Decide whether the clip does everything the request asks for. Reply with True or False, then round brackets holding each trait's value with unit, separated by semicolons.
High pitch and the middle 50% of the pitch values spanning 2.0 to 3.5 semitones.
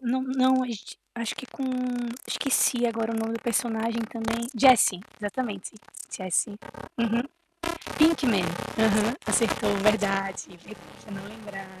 True (225 Hz; 2.8 semitones)